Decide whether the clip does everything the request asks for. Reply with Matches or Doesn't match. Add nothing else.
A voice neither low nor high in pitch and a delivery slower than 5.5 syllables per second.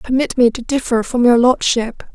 Doesn't match